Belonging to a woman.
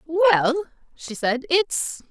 Yes: female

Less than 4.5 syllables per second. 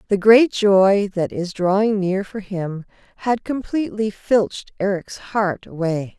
Yes: 4.0 syllables/s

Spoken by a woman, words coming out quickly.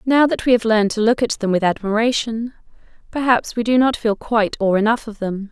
Yes: female; fast, 230 wpm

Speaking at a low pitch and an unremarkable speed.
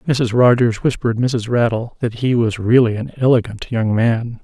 Yes: low, 120 Hz; average, 175 wpm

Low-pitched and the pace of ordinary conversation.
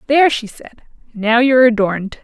No: high, 235 Hz; average, 160 wpm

